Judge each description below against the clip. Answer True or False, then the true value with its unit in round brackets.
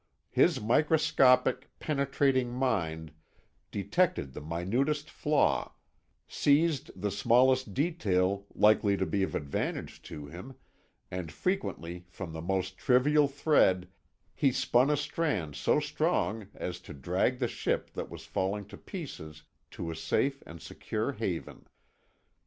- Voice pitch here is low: True (115 Hz)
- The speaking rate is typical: False (130 wpm)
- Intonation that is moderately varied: False (7.8 semitones)